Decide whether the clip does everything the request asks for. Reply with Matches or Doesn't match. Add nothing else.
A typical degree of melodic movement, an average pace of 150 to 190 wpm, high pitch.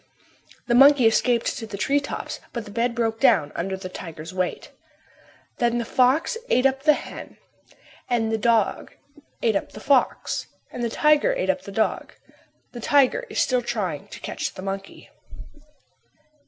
Matches